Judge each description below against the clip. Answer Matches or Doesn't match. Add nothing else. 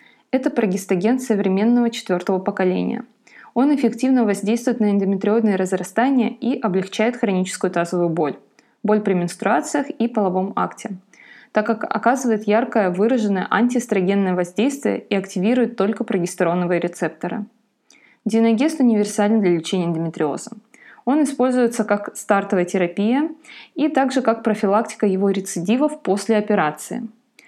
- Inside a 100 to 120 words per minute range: Matches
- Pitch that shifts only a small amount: Doesn't match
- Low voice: Doesn't match